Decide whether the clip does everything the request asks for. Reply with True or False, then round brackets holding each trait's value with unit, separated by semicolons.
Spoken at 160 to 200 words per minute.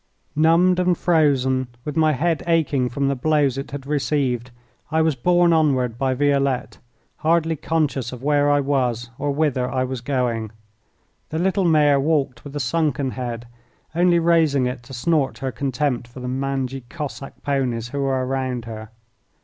True (165 wpm)